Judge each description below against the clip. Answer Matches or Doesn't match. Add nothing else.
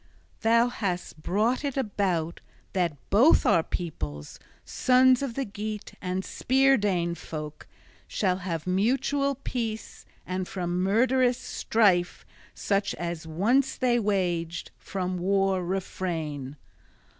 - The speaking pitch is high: Matches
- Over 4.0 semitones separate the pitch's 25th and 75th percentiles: Matches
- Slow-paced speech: Matches